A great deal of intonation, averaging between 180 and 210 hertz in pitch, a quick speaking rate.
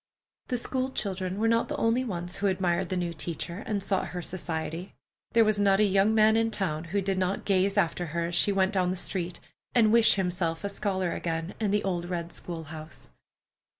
No: average, 2.9 semitones; high, 190 Hz; fast, 215 wpm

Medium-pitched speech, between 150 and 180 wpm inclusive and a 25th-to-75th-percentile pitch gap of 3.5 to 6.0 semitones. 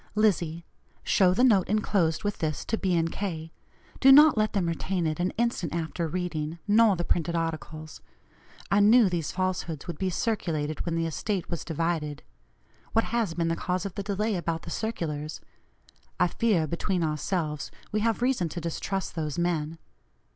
Yes: medium, 175 Hz; average, 175 wpm; average, 4.0 semitones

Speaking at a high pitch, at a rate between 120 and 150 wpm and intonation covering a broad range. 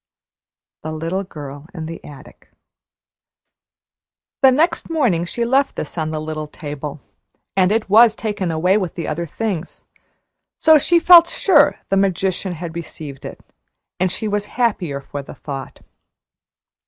No: medium, 180 Hz; average, 145 wpm; wide, 6.2 semitones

